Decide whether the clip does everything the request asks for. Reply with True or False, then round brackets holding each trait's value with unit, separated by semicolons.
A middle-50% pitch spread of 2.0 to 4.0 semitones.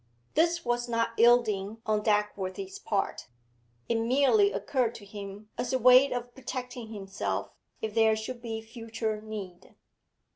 True (2.8 semitones)